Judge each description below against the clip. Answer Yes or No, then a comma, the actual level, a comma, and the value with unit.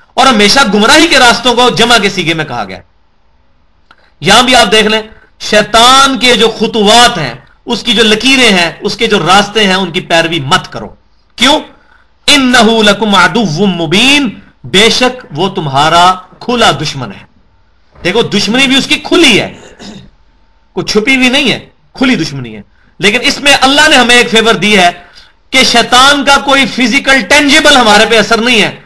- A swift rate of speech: No, average, 175 wpm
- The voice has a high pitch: Yes, high, 220 Hz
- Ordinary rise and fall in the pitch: No, wide, 5.7 semitones